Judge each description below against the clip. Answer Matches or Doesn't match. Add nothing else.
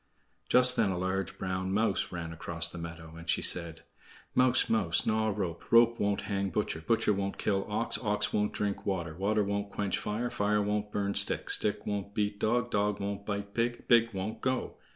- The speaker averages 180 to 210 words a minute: Matches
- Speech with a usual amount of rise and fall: Doesn't match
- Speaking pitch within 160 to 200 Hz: Doesn't match